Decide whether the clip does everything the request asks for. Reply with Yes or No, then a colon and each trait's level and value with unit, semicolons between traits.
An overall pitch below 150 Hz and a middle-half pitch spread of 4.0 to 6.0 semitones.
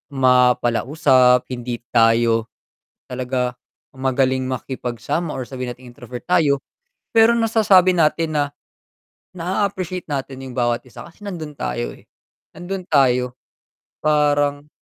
Yes: low, 135 Hz; average, 4.8 semitones